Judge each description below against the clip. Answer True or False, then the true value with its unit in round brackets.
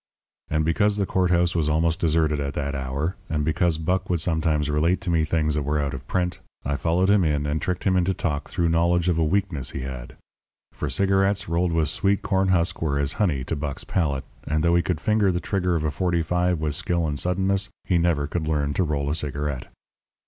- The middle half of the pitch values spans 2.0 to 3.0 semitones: False (3.4 semitones)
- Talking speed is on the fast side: True (230 wpm)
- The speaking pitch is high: False (80 Hz)